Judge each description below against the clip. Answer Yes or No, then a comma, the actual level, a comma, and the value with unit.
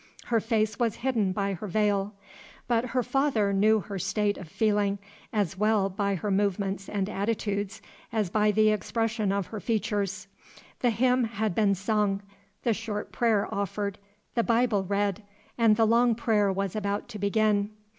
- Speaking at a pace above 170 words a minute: No, average, 165 wpm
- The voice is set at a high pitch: Yes, high, 210 Hz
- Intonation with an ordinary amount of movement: No, narrow, 2.0 semitones